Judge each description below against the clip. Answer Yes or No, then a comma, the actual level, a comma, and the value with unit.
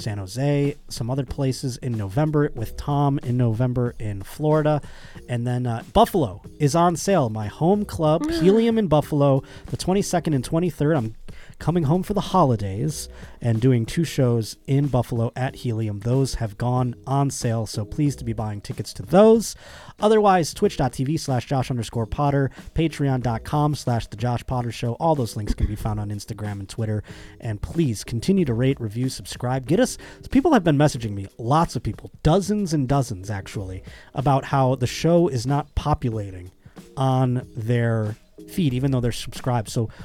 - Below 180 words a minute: Yes, average, 170 wpm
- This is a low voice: Yes, low, 130 Hz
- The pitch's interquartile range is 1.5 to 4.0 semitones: No, average, 5.0 semitones